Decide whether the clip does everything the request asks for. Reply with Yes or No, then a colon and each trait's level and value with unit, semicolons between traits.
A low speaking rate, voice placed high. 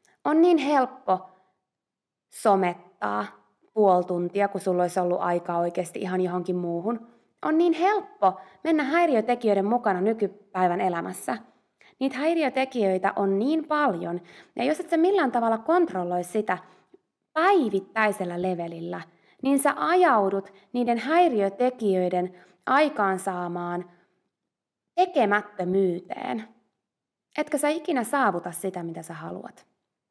No: average, 105 wpm; high, 200 Hz